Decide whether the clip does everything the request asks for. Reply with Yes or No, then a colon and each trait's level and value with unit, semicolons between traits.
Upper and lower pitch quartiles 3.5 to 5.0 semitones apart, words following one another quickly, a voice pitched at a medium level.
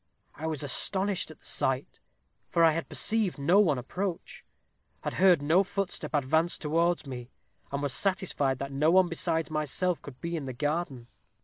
No: average, 4.1 semitones; average, 175 wpm; medium, 160 Hz